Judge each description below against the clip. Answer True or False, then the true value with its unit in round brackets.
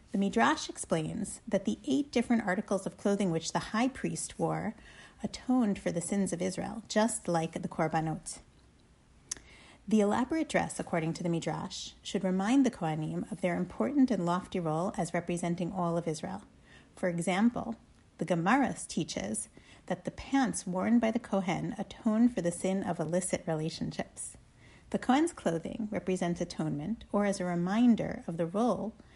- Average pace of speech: True (160 wpm)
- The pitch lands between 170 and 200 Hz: True (190 Hz)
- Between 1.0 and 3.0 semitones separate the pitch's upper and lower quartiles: False (4.2 semitones)